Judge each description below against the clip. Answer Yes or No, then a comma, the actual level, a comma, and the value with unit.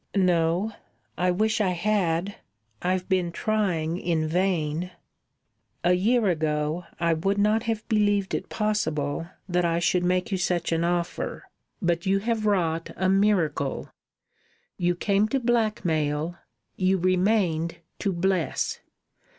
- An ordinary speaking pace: No, slow, 130 wpm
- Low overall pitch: No, medium, 180 Hz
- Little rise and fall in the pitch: No, average, 3.3 semitones